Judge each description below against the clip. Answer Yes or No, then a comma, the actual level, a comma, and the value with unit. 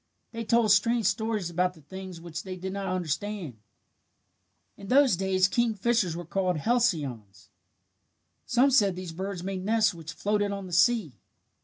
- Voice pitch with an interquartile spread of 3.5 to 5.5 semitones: Yes, average, 4.0 semitones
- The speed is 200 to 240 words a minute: No, average, 155 wpm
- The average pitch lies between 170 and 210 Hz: Yes, high, 190 Hz